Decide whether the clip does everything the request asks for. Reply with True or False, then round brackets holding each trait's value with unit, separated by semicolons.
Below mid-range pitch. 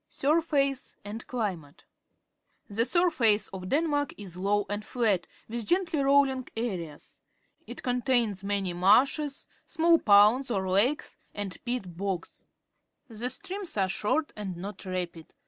False (220 Hz)